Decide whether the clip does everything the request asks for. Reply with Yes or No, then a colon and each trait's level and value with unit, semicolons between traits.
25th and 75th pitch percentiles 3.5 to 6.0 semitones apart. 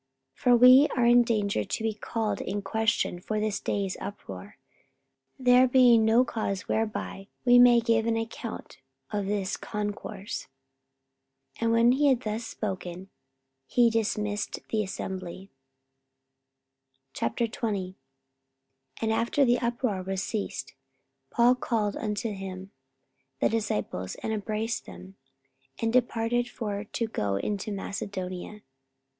No: average, 3.0 semitones